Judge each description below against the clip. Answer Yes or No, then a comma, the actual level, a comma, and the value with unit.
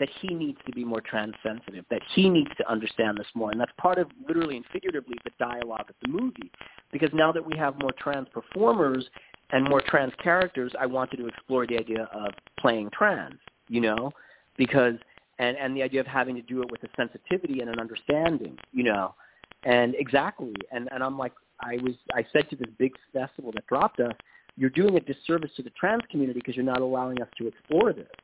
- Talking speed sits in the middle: No, fast, 215 wpm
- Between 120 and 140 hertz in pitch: Yes, low, 130 Hz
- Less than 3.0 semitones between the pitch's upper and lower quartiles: No, average, 3.6 semitones